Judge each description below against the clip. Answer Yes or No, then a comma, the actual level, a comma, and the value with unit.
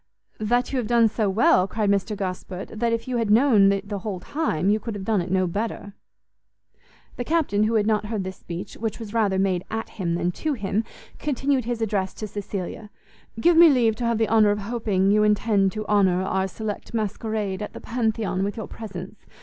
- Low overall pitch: No, high, 210 Hz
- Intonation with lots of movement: No, average, 2.8 semitones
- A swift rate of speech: Yes, fast, 215 wpm